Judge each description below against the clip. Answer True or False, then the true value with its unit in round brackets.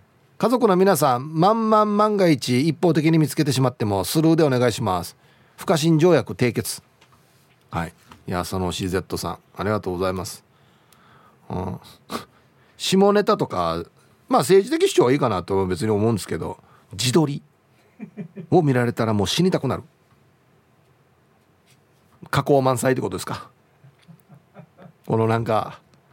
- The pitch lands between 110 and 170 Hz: True (135 Hz)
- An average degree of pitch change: False (7.0 semitones)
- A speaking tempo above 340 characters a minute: False (280 characters per minute)